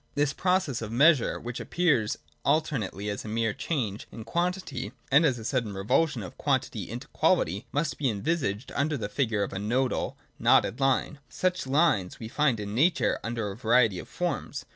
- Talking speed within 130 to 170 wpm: No, average, 180 wpm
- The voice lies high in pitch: No, low, 125 Hz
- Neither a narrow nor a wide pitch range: No, wide, 5.8 semitones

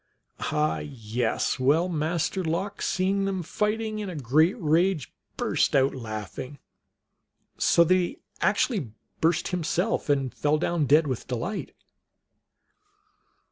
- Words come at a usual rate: No, slow, 120 wpm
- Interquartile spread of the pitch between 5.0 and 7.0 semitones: Yes, wide, 5.4 semitones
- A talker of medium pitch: Yes, medium, 160 Hz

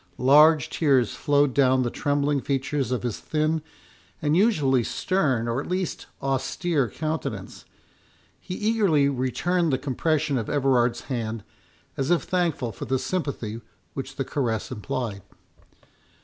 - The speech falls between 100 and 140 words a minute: Yes, slow, 135 wpm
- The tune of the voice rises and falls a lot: No, average, 3.7 semitones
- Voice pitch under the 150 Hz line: Yes, medium, 140 Hz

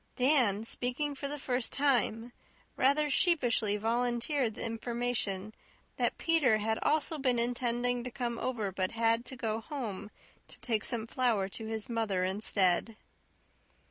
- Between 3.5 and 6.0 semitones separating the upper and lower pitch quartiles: No, average, 2.8 semitones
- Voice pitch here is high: Yes, high, 235 Hz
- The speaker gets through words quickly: No, average, 140 wpm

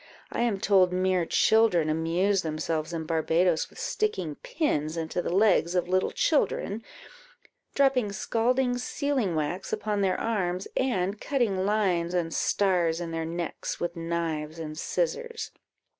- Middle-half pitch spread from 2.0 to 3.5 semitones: No, average, 5.2 semitones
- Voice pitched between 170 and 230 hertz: Yes, medium, 185 Hz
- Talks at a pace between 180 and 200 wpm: No, average, 140 wpm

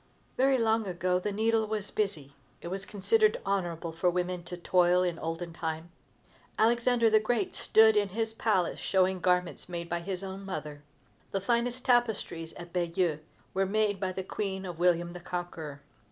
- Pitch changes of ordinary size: Yes, average, 3.9 semitones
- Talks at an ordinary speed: Yes, average, 170 wpm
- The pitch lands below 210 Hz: Yes, medium, 185 Hz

